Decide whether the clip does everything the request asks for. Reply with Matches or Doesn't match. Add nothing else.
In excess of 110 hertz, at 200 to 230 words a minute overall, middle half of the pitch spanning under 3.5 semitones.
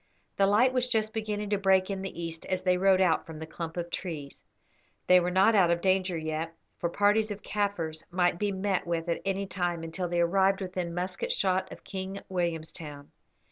Matches